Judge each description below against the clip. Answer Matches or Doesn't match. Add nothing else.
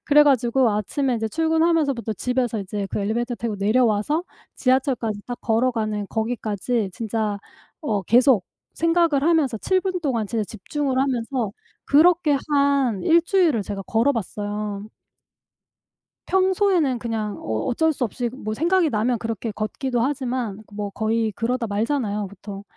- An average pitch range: Matches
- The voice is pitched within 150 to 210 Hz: Doesn't match